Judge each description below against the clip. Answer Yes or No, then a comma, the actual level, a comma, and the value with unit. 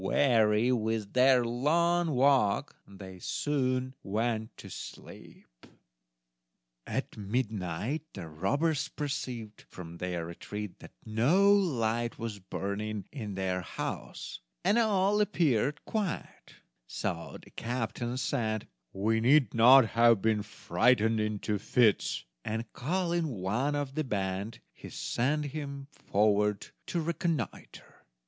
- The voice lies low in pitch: Yes, low, 115 Hz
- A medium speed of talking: No, slow, 115 wpm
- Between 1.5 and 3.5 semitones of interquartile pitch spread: No, wide, 5.4 semitones